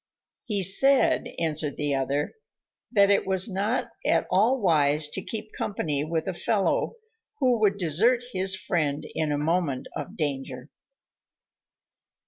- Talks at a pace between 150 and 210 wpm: No, slow, 135 wpm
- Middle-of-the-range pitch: Yes, medium, 180 Hz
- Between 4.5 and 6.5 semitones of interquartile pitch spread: Yes, average, 5.3 semitones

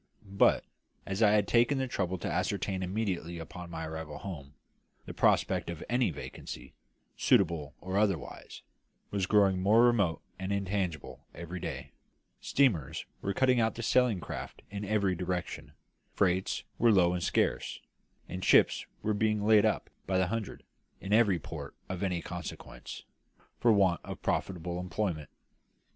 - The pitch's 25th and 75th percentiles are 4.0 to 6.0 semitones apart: No, average, 3.5 semitones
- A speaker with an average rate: Yes, average, 150 wpm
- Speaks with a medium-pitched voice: No, very low, 95 Hz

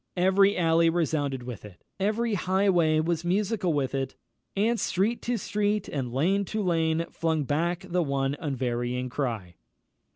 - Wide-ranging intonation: Yes, wide, 6.1 semitones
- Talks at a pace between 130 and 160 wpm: Yes, average, 150 wpm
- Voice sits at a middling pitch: Yes, medium, 165 Hz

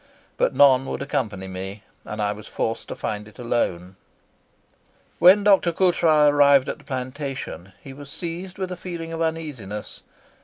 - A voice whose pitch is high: No, medium, 140 Hz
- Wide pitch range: Yes, wide, 7.7 semitones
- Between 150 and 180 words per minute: Yes, average, 160 wpm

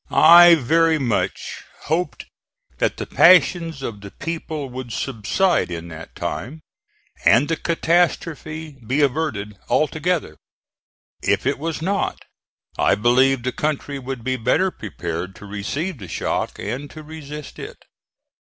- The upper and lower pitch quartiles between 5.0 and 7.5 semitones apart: Yes, wide, 5.6 semitones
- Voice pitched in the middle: Yes, medium, 145 Hz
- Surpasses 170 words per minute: No, slow, 135 wpm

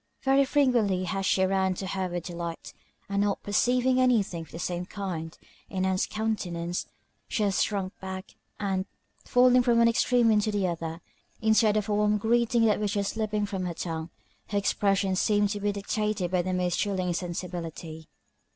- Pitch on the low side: No, high, 200 Hz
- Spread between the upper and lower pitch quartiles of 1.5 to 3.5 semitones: Yes, average, 3.0 semitones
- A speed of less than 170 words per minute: No, average, 180 wpm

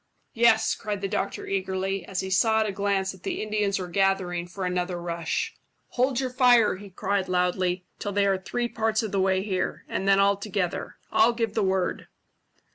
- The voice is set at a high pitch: Yes, high, 195 Hz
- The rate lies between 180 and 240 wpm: Yes, average, 200 wpm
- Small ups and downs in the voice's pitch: Yes, narrow, 2.3 semitones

